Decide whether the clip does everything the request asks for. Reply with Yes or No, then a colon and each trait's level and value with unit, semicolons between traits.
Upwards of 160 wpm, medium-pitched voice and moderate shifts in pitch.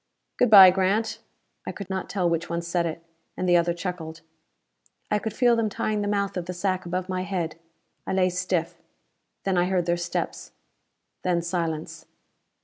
No: average, 180 wpm; medium, 180 Hz; narrow, 2.1 semitones